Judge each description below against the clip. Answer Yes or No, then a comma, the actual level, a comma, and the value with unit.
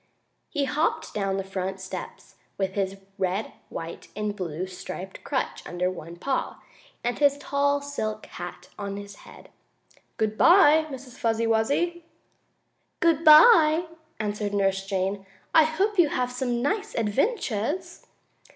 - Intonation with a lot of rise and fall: Yes, wide, 7.7 semitones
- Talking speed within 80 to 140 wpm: Yes, slow, 135 wpm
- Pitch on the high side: Yes, high, 225 Hz